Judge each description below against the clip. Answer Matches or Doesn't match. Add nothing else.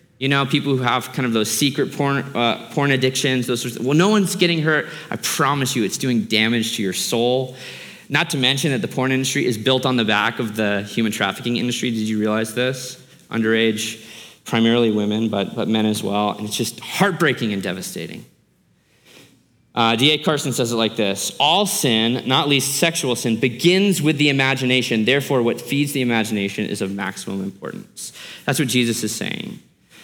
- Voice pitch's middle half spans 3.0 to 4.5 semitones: Matches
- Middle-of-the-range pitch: Doesn't match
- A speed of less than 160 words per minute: Doesn't match